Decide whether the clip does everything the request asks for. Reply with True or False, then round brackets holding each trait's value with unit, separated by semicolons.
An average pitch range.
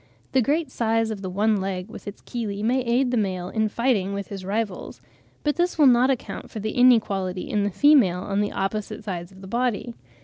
True (4.0 semitones)